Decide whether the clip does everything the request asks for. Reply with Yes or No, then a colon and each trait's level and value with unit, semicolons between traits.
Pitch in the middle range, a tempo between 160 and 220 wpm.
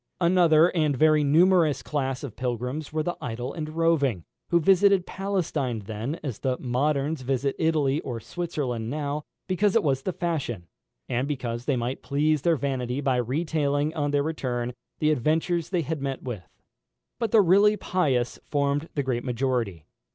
Yes: medium, 145 Hz; average, 165 wpm